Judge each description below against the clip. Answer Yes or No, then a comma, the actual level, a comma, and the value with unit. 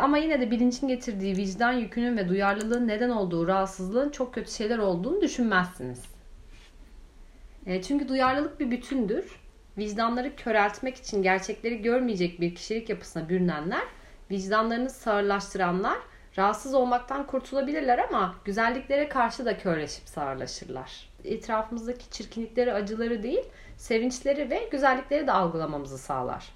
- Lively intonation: No, average, 4.7 semitones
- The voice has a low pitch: No, high, 230 Hz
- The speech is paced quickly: No, average, 115 wpm